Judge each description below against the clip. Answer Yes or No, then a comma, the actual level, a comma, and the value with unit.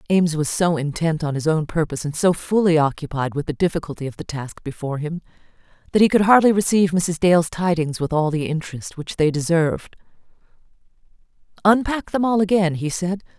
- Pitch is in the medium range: Yes, medium, 170 Hz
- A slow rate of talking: No, average, 185 wpm